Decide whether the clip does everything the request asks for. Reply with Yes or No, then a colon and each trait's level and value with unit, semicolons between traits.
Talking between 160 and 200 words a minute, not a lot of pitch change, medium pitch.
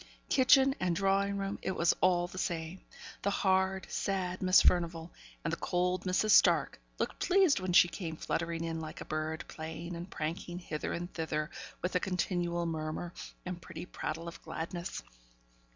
Yes: average, 170 wpm; narrow, 2.3 semitones; medium, 175 Hz